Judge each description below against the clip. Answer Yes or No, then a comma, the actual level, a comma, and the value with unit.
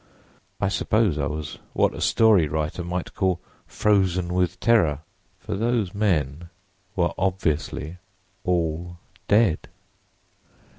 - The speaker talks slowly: Yes, slow, 110 wpm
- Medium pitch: No, very low, 90 Hz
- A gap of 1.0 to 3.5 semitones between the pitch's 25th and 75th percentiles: No, average, 4.2 semitones